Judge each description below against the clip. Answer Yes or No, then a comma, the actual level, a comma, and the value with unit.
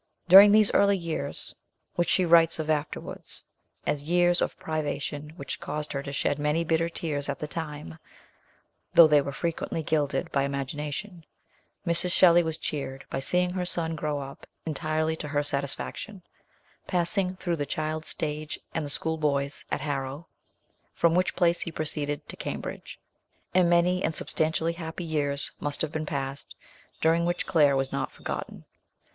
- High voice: No, medium, 155 Hz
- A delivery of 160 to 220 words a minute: Yes, average, 165 wpm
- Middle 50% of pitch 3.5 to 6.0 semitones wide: No, average, 2.8 semitones